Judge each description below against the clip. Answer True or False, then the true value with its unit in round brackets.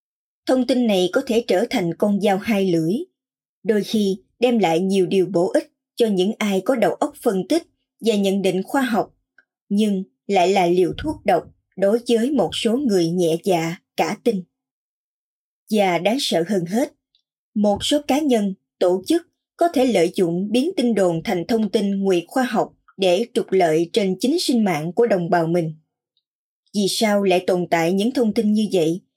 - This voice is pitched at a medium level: False (205 Hz)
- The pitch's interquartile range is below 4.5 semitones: False (5.1 semitones)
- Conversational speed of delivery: True (190 wpm)